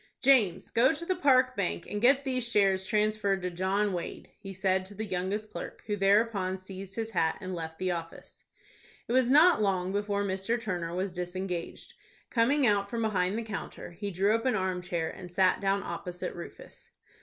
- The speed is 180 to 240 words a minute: Yes, average, 190 wpm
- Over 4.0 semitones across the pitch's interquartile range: No, average, 3.5 semitones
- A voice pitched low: No, high, 195 Hz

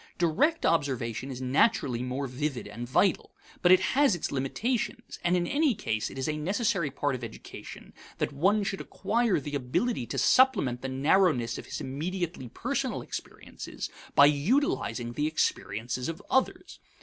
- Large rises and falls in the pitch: Yes, wide, 7.2 semitones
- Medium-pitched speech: Yes, medium, 150 Hz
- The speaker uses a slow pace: No, average, 160 wpm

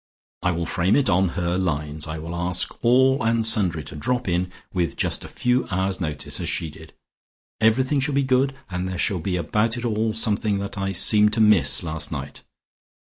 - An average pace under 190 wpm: No, fast, 205 wpm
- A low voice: Yes, very low, 95 Hz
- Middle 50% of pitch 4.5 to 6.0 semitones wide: Yes, average, 4.9 semitones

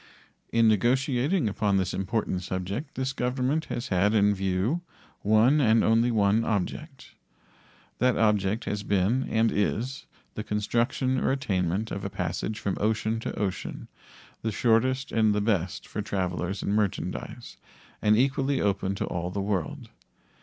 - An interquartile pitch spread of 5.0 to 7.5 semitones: No, average, 3.7 semitones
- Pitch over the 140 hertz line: No, low, 110 Hz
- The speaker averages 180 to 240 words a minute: No, average, 145 wpm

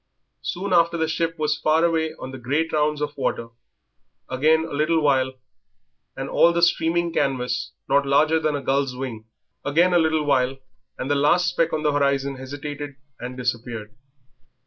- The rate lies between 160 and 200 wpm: Yes, average, 170 wpm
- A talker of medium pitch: Yes, medium, 145 Hz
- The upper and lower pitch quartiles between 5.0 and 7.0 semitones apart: No, average, 3.3 semitones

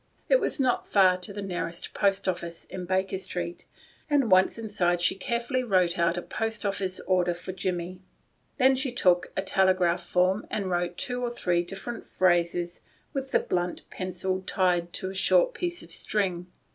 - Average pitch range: Yes, average, 3.4 semitones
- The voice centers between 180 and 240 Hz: Yes, medium, 185 Hz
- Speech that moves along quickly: No, average, 175 wpm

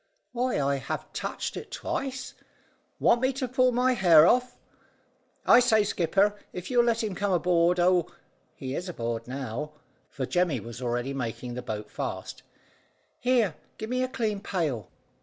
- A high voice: No, medium, 180 Hz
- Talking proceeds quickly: No, average, 160 wpm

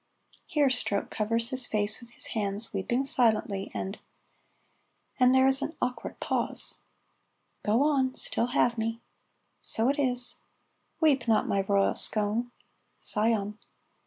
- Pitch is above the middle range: Yes, high, 235 Hz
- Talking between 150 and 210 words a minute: No, slow, 135 wpm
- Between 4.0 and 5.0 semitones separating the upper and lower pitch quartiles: No, average, 3.5 semitones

